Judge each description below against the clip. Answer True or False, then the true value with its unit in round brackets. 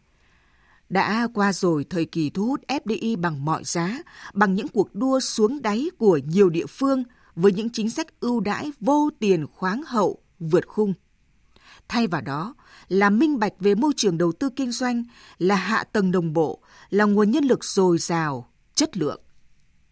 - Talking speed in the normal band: True (180 wpm)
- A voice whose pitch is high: True (205 Hz)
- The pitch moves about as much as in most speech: False (5.7 semitones)